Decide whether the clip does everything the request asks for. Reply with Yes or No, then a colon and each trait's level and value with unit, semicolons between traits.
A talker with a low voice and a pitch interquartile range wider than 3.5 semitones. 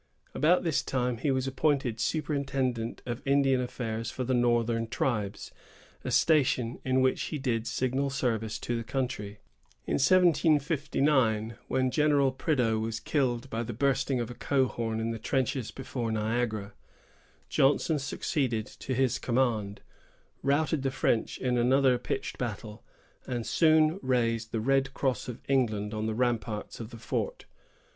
No: low, 125 Hz; average, 3.0 semitones